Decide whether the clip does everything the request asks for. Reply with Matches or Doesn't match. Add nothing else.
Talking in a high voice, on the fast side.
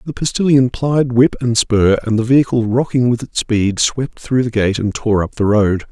Doesn't match